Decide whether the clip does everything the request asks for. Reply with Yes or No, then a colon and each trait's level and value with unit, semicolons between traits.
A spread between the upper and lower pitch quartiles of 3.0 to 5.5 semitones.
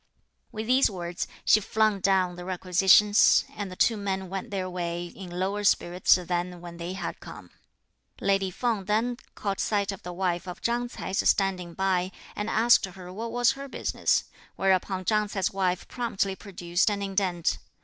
No: narrow, 2.5 semitones